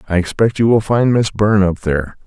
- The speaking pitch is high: No, low, 100 Hz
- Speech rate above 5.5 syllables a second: Yes, 6.0 syllables/s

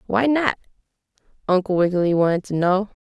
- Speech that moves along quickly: No, average, 140 wpm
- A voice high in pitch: Yes, high, 195 Hz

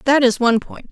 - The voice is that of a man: No, female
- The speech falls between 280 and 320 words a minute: No, fast, 260 wpm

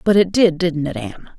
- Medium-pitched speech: Yes, medium, 170 Hz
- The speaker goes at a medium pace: No, fast, 260 wpm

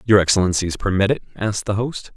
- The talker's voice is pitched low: Yes, low, 100 Hz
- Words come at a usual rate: Yes, average, 195 wpm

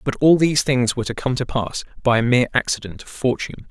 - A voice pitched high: No, low, 125 Hz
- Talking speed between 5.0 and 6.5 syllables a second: No, 7.0 syllables/s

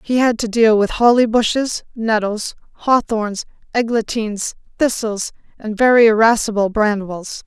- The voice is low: No, high, 220 Hz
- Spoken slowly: Yes, slow, 120 wpm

